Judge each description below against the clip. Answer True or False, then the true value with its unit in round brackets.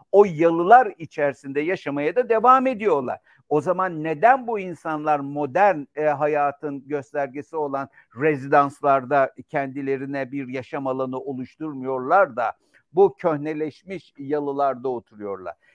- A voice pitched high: False (145 Hz)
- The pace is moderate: True (105 wpm)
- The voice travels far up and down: False (3.4 semitones)